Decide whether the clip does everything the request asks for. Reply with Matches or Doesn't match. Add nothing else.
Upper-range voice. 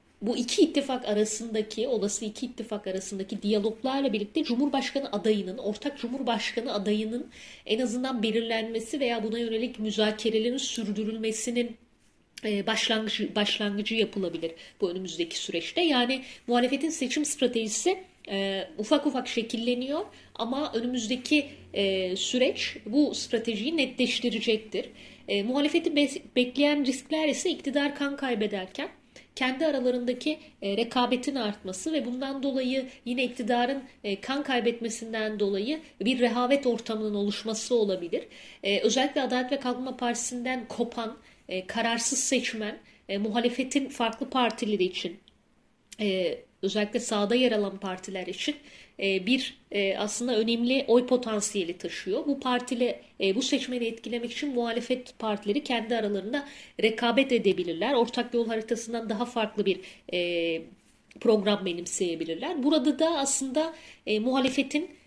Matches